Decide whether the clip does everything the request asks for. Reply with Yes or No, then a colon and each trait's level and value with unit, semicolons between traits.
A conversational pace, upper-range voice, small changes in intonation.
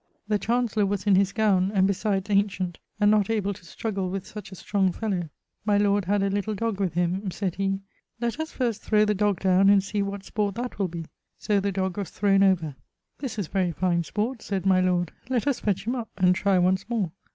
No: fast, 225 wpm; high, 200 Hz; narrow, 2.0 semitones